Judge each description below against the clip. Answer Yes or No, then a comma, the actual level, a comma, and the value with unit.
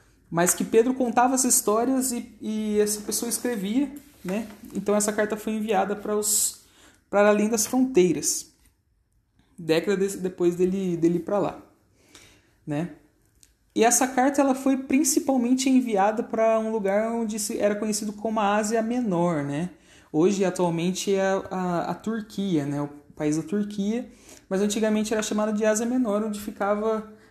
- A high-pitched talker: Yes, high, 210 Hz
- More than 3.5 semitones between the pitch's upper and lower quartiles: Yes, average, 4.2 semitones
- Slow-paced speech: No, average, 155 wpm